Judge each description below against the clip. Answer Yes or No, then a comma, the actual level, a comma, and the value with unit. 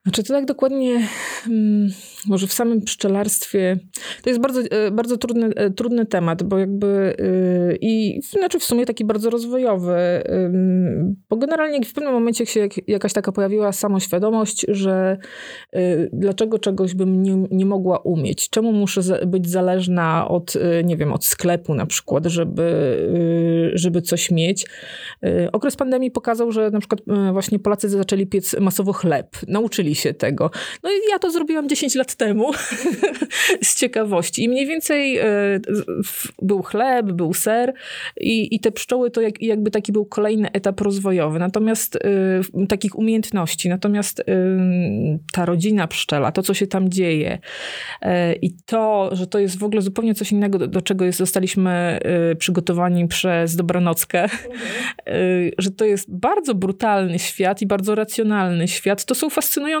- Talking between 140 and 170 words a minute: Yes, average, 150 wpm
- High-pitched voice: Yes, high, 200 Hz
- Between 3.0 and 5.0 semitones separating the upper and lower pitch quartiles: Yes, average, 3.6 semitones